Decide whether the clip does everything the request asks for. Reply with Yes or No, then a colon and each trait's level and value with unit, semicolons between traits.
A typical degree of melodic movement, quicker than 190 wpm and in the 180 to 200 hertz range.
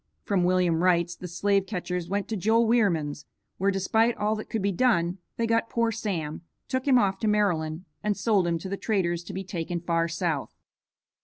Yes: average, 3.9 semitones; average, 200 wpm; high, 190 Hz